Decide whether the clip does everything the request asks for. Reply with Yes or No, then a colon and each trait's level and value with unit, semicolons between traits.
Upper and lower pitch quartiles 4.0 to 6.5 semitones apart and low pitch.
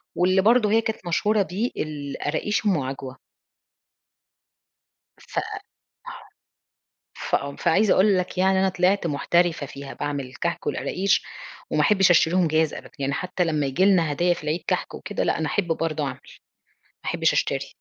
No: average, 4.5 semitones; medium, 175 Hz